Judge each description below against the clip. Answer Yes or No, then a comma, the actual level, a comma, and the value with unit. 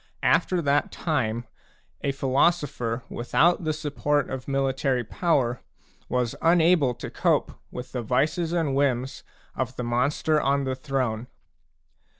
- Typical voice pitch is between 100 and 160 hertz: Yes, low, 135 Hz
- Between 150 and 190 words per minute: No, slow, 135 wpm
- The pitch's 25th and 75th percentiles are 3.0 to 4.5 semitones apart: Yes, average, 3.4 semitones